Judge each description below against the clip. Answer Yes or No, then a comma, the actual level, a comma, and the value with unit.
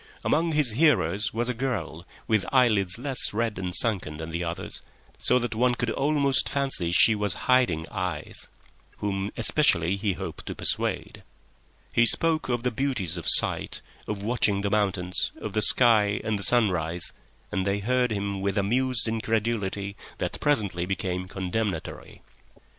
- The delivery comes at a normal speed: Yes, average, 155 wpm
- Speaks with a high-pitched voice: No, low, 105 Hz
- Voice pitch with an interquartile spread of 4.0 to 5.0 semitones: Yes, average, 4.5 semitones